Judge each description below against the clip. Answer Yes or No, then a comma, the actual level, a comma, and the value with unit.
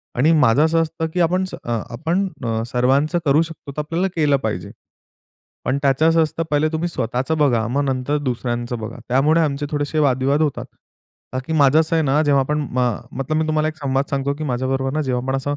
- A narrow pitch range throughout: No, average, 3.2 semitones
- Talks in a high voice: No, medium, 145 Hz